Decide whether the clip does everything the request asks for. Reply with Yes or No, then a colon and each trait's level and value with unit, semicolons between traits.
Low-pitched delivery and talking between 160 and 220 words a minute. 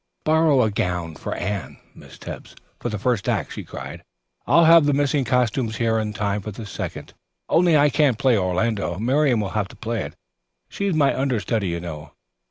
Yes: low, 115 Hz; average, 190 wpm